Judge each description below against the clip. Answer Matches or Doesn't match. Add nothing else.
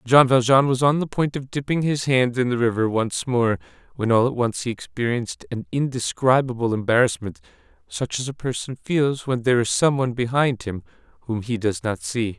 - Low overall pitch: Matches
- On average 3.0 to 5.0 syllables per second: Doesn't match